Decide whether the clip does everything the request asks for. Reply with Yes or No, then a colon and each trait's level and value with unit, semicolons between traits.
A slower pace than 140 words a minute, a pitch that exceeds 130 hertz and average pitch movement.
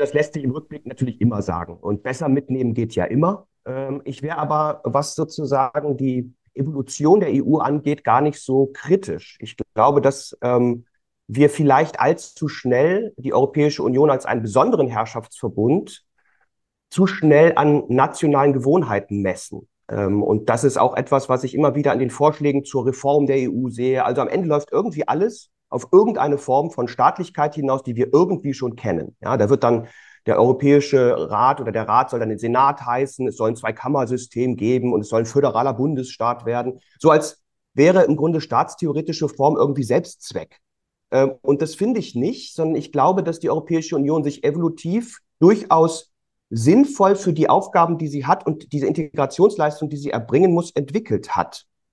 No: average, 170 wpm; medium, 140 Hz; average, 3.4 semitones